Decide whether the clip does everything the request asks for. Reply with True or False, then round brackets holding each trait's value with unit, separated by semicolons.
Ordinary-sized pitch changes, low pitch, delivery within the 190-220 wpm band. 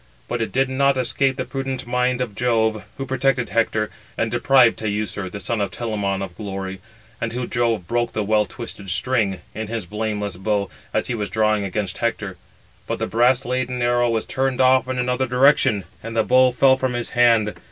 True (3.3 semitones; 115 Hz; 195 wpm)